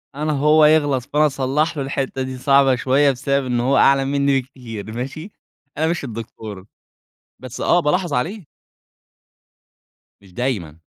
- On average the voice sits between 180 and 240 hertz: No, low, 135 Hz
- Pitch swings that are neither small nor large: Yes, average, 3.1 semitones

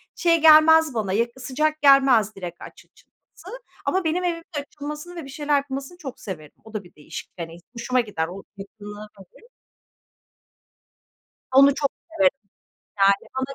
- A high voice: Yes, very high, 270 Hz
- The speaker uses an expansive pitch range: Yes, wide, 7.0 semitones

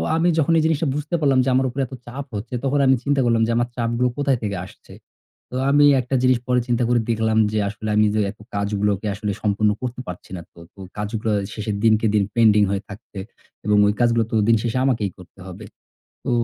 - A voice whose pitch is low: Yes, low, 115 Hz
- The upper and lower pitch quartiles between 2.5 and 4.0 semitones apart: Yes, average, 3.7 semitones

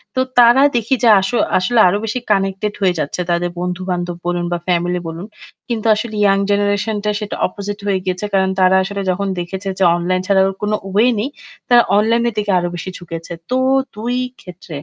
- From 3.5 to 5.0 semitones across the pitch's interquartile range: No, average, 2.8 semitones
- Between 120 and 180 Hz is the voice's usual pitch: No, high, 195 Hz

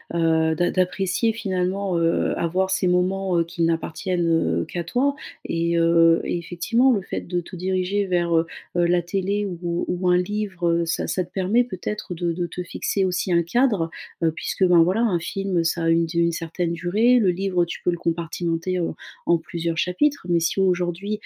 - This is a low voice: No, medium, 175 Hz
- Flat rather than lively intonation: Yes, narrow, 2.2 semitones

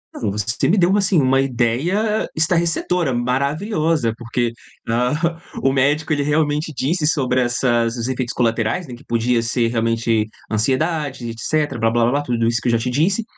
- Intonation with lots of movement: No, average, 5.0 semitones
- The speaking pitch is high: No, low, 130 Hz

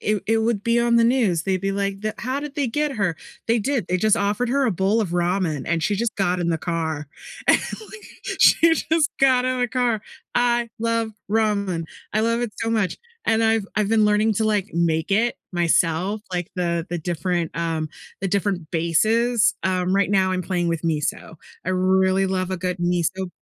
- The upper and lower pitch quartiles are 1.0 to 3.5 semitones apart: No, average, 4.5 semitones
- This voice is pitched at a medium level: No, high, 195 Hz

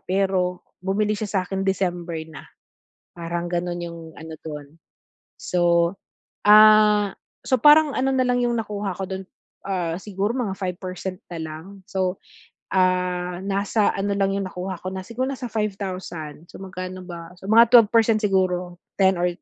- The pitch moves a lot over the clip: No, average, 2.9 semitones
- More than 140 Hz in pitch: Yes, high, 190 Hz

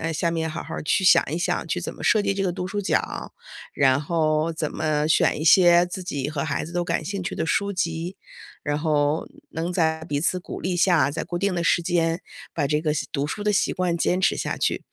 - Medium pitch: Yes, medium, 165 Hz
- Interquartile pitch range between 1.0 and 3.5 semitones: Yes, average, 2.8 semitones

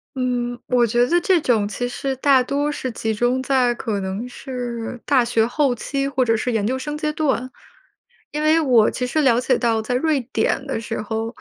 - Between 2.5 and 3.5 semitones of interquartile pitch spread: Yes, average, 2.9 semitones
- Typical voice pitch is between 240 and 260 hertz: Yes, very high, 250 Hz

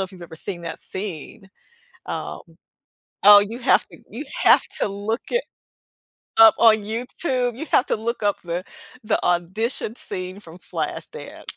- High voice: Yes, high, 205 Hz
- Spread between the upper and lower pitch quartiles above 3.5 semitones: Yes, average, 4.4 semitones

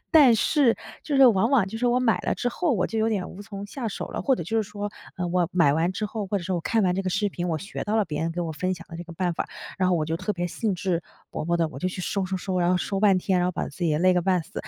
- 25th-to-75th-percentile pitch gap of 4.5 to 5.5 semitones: No, average, 3.6 semitones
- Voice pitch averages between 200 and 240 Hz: No, medium, 185 Hz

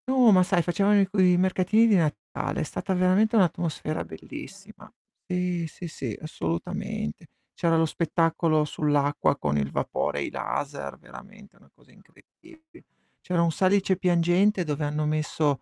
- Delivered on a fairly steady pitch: No, average, 4.0 semitones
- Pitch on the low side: No, medium, 175 Hz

